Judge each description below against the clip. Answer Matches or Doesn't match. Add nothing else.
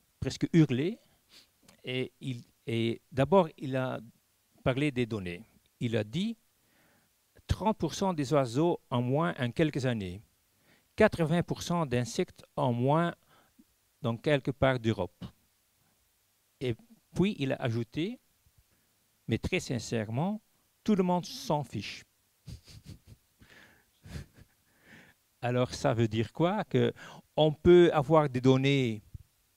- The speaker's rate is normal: Doesn't match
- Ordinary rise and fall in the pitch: Doesn't match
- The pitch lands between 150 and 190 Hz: Doesn't match